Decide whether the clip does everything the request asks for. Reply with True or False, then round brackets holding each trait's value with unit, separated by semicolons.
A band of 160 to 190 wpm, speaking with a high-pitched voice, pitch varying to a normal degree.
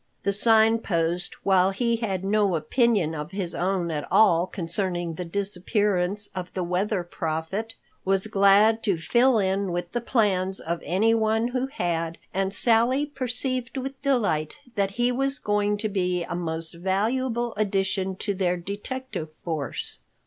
False (150 wpm; 195 Hz; 4.2 semitones)